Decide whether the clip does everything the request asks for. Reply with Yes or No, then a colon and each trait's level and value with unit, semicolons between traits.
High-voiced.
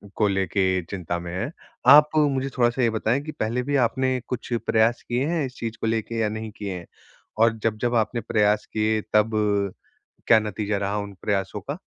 No: low, 110 Hz